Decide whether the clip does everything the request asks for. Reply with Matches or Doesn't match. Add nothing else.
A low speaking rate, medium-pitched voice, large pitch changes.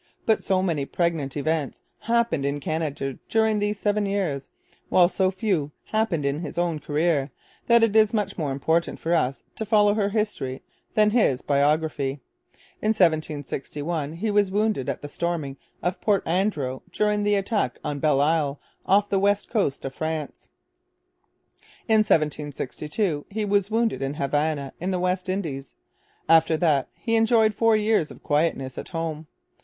Doesn't match